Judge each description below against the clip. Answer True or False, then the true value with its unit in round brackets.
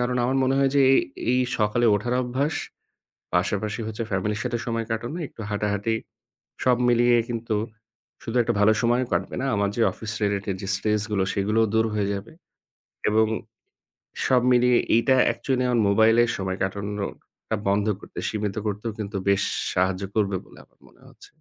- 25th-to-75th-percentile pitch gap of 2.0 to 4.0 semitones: True (2.9 semitones)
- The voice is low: True (110 Hz)